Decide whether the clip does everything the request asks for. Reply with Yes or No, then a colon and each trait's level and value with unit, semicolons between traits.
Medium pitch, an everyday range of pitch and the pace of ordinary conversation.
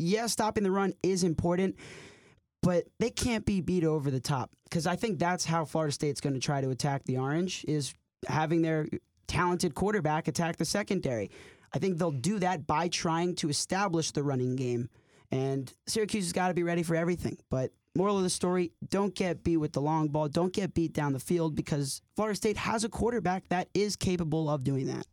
No: medium, 170 Hz; average, 4.0 semitones; fast, 210 wpm